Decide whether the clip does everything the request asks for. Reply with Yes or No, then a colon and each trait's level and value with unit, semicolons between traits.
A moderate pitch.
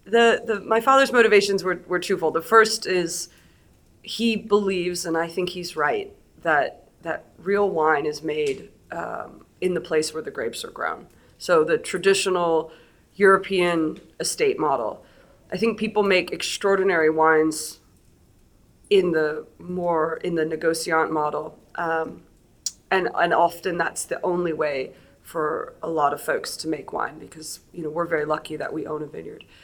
Yes: medium, 175 Hz